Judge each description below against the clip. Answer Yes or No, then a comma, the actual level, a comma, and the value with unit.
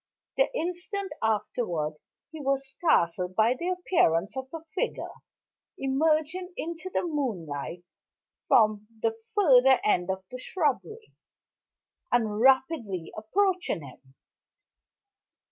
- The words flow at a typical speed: No, slow, 105 wpm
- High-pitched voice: Yes, very high, 265 Hz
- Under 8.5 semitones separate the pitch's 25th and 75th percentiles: No, wide, 8.9 semitones